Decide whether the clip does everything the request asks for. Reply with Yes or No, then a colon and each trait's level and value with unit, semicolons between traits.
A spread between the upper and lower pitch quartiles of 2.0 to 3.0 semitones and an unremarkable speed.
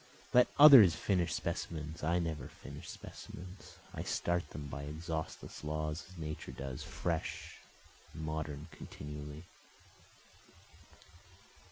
No: narrow, 2.6 semitones; slow, 110 wpm